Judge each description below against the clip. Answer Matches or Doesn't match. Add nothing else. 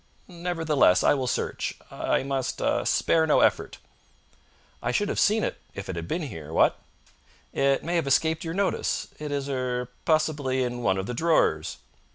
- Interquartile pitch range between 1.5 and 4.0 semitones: Doesn't match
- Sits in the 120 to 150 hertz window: Matches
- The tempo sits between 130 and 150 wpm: Doesn't match